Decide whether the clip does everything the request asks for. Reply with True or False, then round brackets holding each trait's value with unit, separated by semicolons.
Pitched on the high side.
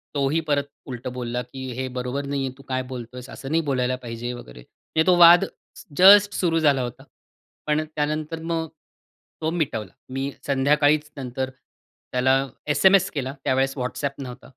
False (135 Hz)